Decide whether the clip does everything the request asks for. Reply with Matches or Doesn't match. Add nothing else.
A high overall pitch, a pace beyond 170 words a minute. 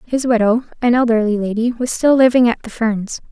Matches